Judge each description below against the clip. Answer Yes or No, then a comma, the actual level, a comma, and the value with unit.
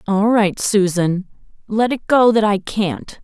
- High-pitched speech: Yes, high, 205 Hz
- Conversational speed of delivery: Yes, average, 165 wpm